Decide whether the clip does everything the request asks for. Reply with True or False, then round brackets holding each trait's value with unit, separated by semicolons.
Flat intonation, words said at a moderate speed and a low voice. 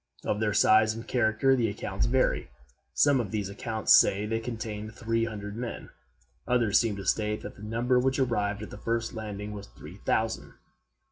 True (1.9 semitones; 185 wpm; 110 Hz)